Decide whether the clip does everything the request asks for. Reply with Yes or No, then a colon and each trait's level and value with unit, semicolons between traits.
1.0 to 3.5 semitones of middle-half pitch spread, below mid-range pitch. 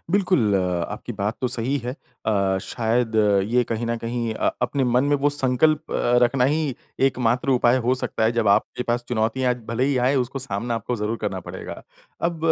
Yes: average, 2.8 semitones; low, 120 Hz